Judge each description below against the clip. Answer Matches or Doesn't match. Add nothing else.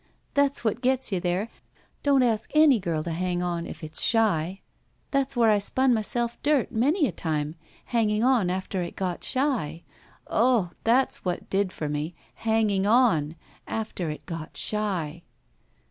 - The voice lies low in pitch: Doesn't match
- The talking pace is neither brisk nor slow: Matches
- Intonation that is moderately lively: Doesn't match